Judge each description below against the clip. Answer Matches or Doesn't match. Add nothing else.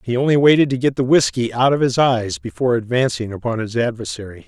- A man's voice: Matches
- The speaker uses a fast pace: Matches